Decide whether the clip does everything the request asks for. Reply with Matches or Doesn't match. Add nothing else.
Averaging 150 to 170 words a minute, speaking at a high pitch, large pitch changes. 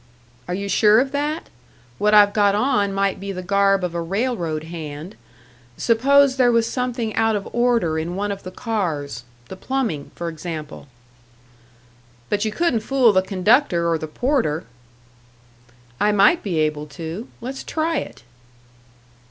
Matches